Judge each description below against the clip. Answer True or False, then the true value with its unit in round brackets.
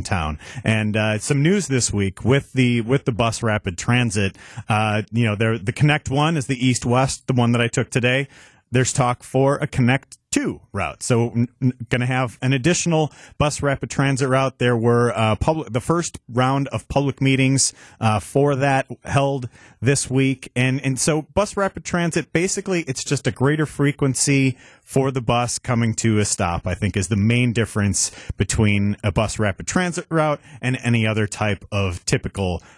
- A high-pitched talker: False (125 Hz)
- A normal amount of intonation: True (3.9 semitones)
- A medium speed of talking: True (185 wpm)